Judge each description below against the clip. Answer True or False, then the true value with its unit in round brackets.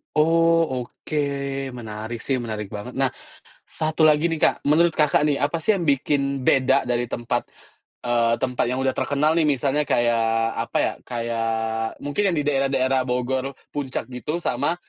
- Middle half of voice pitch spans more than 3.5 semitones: True (4.0 semitones)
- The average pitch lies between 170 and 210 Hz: False (135 Hz)